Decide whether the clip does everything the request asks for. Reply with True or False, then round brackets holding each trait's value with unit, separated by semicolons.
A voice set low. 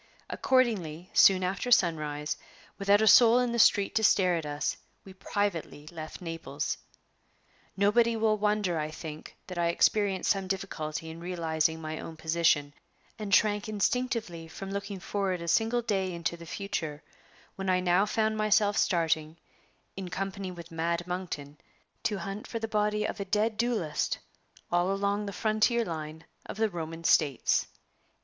False (190 Hz)